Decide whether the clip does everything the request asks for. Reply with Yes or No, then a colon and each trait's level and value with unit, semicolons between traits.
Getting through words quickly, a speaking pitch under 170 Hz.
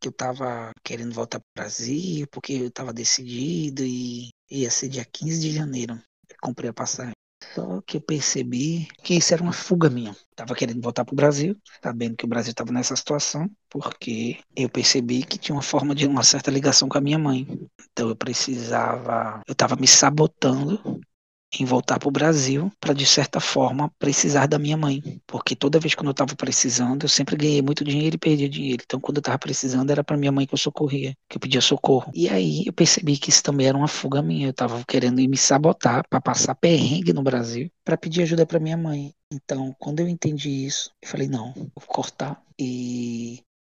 Yes: fast, 210 wpm; low, 135 Hz